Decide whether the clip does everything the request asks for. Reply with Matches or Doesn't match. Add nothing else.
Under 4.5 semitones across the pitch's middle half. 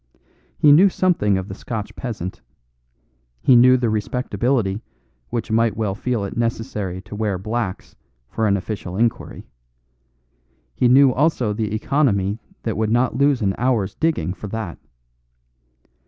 Matches